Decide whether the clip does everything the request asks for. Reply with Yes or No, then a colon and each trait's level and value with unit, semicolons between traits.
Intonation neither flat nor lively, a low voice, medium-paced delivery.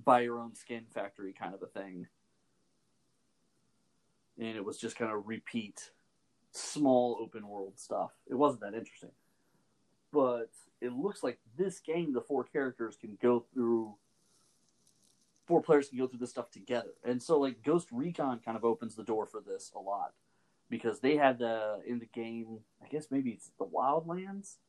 Yes: average, 3.6 semitones; low, 120 Hz; average, 175 wpm